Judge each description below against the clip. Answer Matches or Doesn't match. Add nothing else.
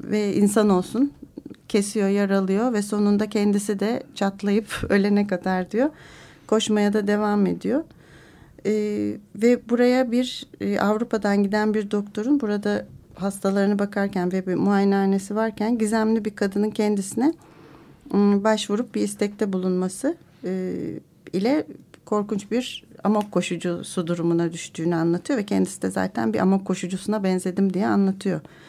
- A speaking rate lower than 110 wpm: Doesn't match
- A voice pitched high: Matches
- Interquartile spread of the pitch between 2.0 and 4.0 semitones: Matches